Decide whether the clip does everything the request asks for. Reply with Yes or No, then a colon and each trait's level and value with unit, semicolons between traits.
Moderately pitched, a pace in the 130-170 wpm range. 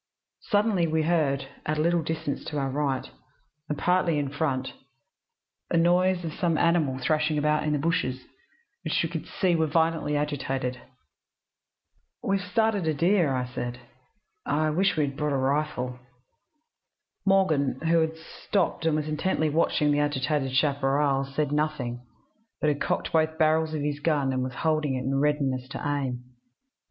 Yes: medium, 150 Hz; average, 165 wpm